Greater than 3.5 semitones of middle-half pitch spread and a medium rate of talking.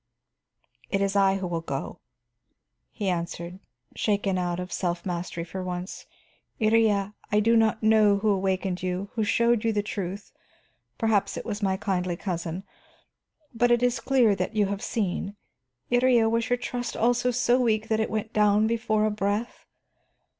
No: average, 3.1 semitones; average, 165 wpm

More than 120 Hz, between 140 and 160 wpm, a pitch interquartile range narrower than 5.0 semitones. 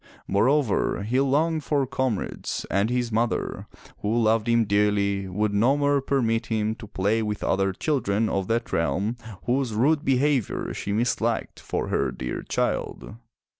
No: low, 115 Hz; average, 150 wpm; average, 4.3 semitones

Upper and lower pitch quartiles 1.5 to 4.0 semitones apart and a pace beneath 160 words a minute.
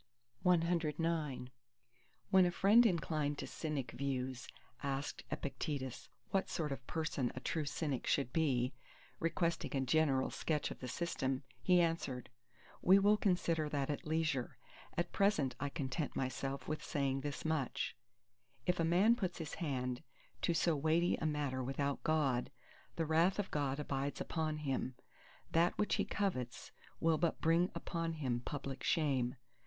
Yes: average, 3.7 semitones; average, 150 wpm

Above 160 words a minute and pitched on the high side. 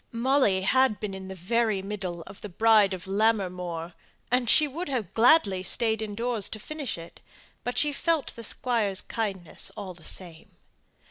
Yes: average, 170 wpm; high, 210 Hz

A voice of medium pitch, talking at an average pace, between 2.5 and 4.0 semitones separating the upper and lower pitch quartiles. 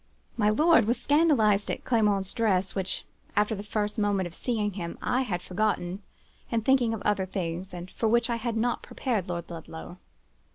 No: high, 210 Hz; average, 180 wpm; average, 3.7 semitones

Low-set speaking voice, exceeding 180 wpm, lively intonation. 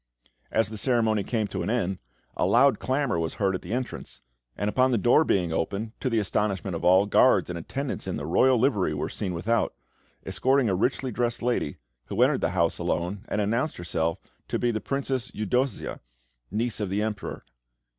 No: low, 105 Hz; average, 195 wpm; average, 4.9 semitones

